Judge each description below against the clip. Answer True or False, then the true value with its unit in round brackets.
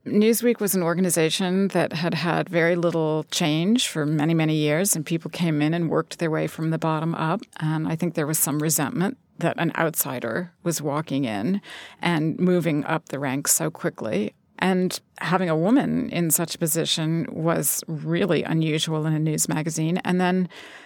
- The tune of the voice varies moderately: False (2.3 semitones)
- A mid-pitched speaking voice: True (165 Hz)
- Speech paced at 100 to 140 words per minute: False (180 wpm)